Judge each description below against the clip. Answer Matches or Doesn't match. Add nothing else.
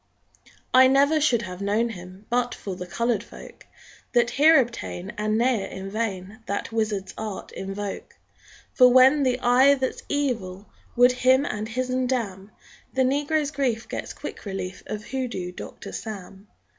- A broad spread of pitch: Doesn't match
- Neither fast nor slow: Matches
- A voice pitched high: Matches